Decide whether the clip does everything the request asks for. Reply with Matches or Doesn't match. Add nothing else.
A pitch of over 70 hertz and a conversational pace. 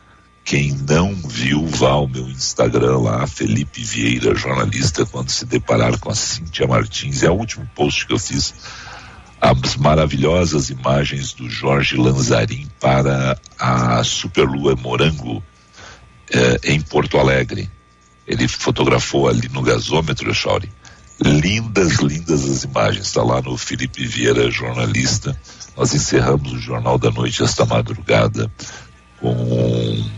Doesn't match